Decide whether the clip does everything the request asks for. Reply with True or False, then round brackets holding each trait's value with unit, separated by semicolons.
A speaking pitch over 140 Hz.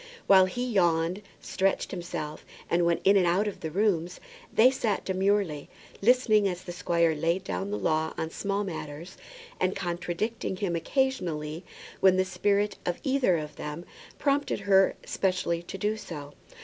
True (185 Hz)